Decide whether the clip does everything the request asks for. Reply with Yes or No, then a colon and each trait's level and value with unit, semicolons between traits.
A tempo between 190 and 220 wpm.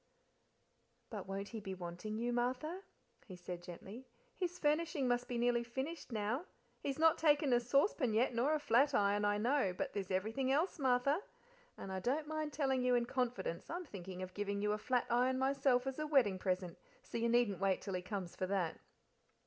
Yes: average, 195 wpm